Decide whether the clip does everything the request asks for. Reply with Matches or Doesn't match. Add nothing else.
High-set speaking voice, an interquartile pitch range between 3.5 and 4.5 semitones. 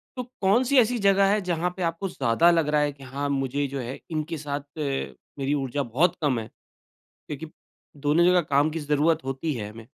Doesn't match